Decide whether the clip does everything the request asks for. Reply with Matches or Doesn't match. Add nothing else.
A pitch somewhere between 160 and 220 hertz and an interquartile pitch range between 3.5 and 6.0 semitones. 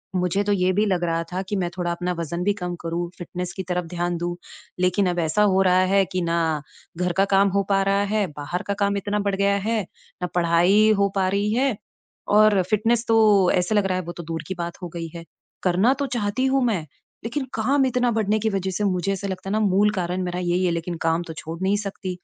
Doesn't match